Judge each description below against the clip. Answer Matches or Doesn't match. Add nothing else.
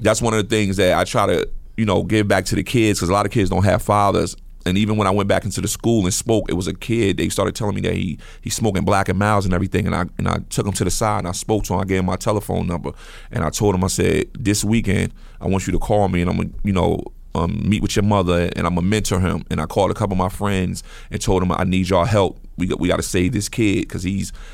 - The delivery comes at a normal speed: Doesn't match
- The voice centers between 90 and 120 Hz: Matches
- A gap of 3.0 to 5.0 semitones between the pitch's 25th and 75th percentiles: Doesn't match